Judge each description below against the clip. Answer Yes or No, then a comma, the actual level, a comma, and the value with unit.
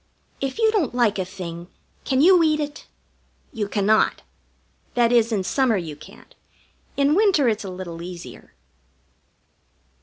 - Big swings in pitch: Yes, wide, 7.5 semitones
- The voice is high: Yes, high, 230 Hz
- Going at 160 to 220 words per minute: No, average, 145 wpm